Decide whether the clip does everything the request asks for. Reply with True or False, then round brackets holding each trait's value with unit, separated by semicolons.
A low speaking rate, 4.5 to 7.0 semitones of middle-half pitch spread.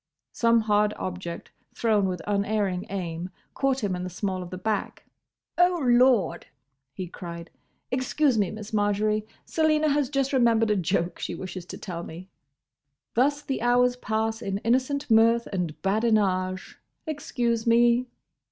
False (145 wpm; 4.8 semitones)